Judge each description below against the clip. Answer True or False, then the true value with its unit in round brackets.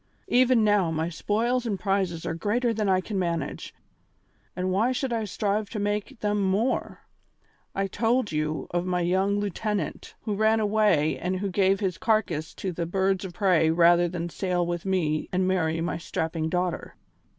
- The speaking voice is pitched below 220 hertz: True (190 Hz)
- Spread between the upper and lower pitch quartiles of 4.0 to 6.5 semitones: False (3.3 semitones)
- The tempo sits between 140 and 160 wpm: False (175 wpm)